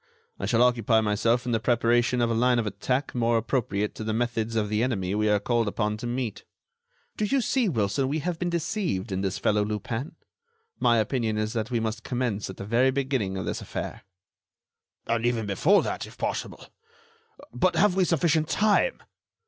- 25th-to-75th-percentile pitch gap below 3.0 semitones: No, average, 3.6 semitones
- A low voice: Yes, low, 115 Hz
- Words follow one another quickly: No, average, 195 wpm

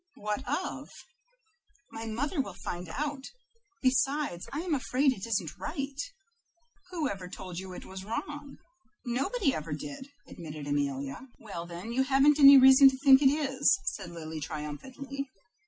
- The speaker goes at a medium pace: Yes, average, 150 wpm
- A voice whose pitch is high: Yes, very high, 255 Hz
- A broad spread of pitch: Yes, wide, 8.2 semitones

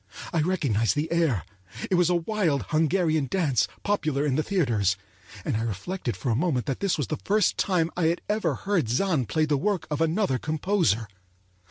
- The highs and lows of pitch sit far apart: Yes, wide, 6.5 semitones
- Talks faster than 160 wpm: Yes, average, 185 wpm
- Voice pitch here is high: No, medium, 155 Hz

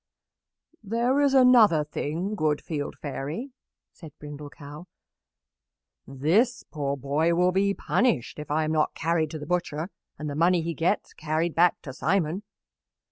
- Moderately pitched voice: Yes, medium, 160 Hz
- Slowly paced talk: No, average, 150 wpm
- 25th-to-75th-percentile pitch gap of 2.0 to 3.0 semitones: No, average, 4.3 semitones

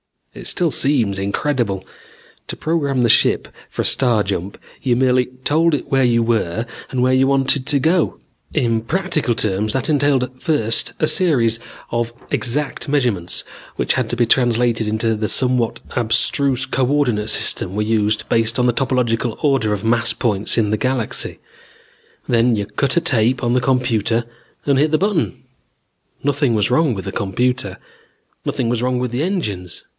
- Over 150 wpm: Yes, average, 170 wpm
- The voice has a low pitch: Yes, low, 125 Hz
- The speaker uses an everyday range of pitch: Yes, average, 3.3 semitones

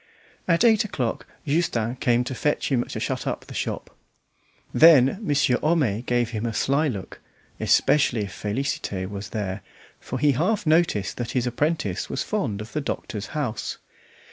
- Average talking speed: Yes, average, 165 wpm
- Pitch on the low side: Yes, low, 125 Hz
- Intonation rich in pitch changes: Yes, wide, 5.9 semitones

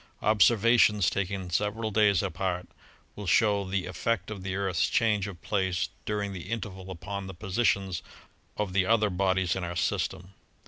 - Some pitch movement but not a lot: No, narrow, 2.2 semitones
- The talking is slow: No, average, 155 wpm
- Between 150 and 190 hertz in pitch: No, very low, 95 Hz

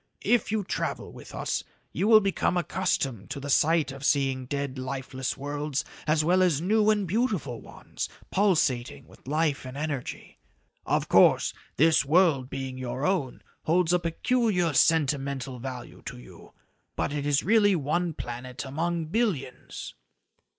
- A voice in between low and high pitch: Yes, medium, 150 Hz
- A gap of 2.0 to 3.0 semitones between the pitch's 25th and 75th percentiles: No, average, 5.1 semitones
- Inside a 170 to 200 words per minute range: No, average, 150 wpm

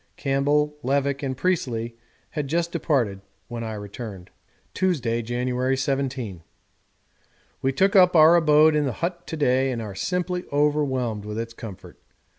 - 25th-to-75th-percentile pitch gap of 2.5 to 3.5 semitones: No, average, 4.7 semitones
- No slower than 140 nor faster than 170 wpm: Yes, average, 145 wpm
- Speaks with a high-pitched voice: No, low, 135 Hz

